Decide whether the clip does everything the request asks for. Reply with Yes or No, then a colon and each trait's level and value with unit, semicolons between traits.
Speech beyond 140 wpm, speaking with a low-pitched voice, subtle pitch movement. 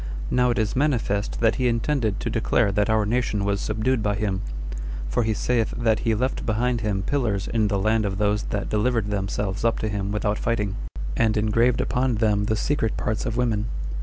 Yes: average, 200 wpm; low, 110 Hz; narrow, 2.3 semitones